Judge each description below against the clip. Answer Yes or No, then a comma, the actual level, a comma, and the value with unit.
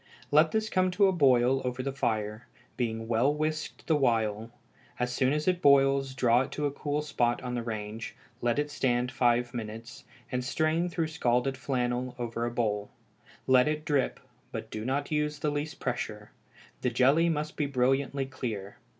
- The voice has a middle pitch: No, low, 130 Hz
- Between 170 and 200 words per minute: Yes, average, 180 wpm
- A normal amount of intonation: Yes, average, 3.6 semitones